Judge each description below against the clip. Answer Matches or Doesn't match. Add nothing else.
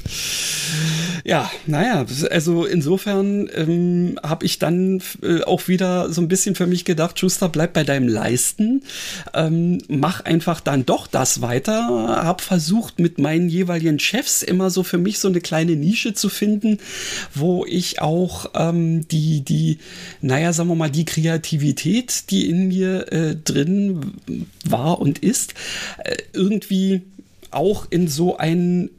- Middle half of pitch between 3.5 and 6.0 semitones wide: Doesn't match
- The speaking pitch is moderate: Matches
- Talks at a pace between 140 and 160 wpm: Matches